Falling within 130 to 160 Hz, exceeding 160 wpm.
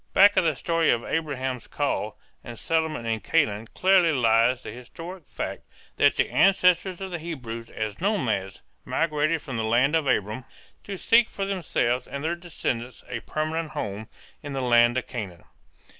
Yes: medium, 140 Hz; average, 170 wpm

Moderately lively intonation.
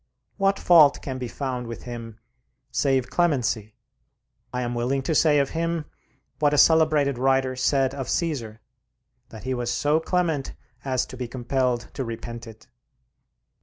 Yes: average, 3.5 semitones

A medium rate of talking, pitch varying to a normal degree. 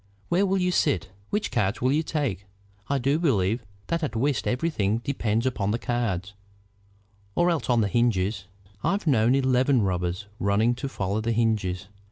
No: average, 170 wpm; wide, 5.8 semitones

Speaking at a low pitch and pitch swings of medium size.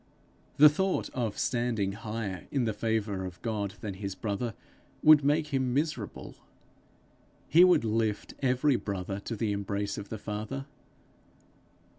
Yes: low, 110 Hz; average, 4.6 semitones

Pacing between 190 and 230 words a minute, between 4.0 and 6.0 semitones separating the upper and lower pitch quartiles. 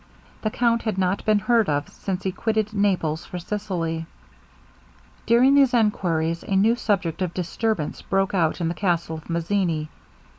No: average, 160 wpm; average, 4.4 semitones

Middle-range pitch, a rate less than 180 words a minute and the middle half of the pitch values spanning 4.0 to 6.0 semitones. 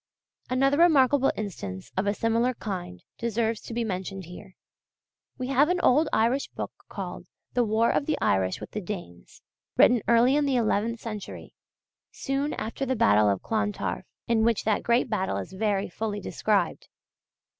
No: high, 225 Hz; average, 165 wpm; average, 4.3 semitones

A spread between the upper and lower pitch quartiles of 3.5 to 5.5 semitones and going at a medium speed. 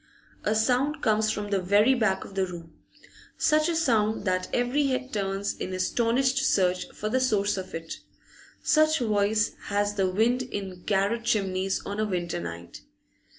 Yes: average, 4.4 semitones; average, 165 wpm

